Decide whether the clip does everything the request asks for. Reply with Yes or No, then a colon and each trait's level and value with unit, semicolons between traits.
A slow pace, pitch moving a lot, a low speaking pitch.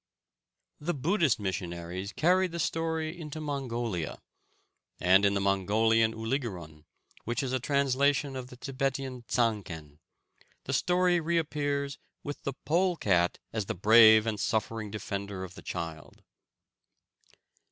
Yes: slow, 125 wpm; wide, 6.5 semitones; low, 120 Hz